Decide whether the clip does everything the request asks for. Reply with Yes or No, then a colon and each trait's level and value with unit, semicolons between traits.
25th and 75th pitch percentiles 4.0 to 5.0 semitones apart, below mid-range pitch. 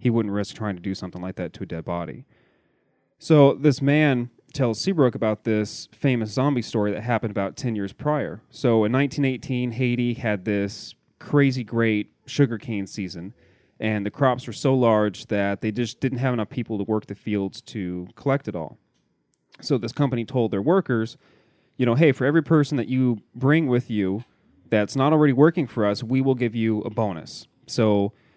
Yes: average, 4.3 semitones; low, 115 Hz